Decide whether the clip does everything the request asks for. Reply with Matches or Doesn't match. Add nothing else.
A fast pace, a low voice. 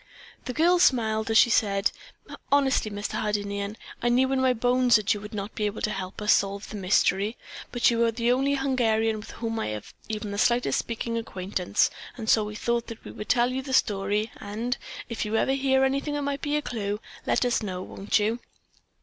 Doesn't match